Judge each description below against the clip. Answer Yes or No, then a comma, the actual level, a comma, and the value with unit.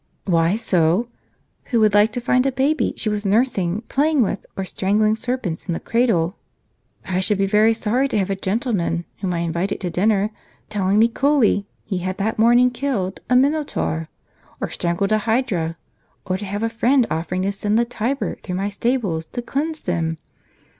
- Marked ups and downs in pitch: No, average, 4.5 semitones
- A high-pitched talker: Yes, high, 210 Hz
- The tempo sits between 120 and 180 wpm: No, average, 190 wpm